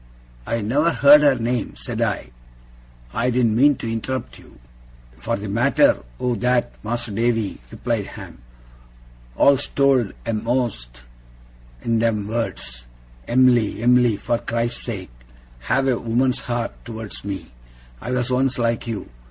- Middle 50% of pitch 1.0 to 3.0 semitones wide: Yes, narrow, 2.6 semitones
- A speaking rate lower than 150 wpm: Yes, slow, 135 wpm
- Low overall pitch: Yes, low, 120 Hz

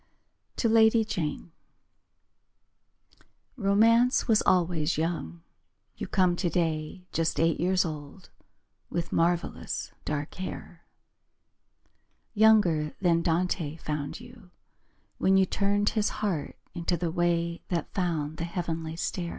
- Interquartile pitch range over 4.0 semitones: No, average, 3.3 semitones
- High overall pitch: No, medium, 175 Hz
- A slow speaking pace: Yes, slow, 110 wpm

